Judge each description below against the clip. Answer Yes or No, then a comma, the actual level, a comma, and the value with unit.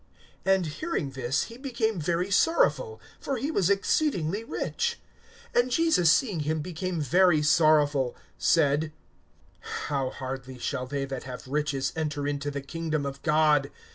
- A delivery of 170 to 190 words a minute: No, average, 140 wpm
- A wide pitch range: Yes, wide, 5.7 semitones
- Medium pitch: Yes, medium, 155 Hz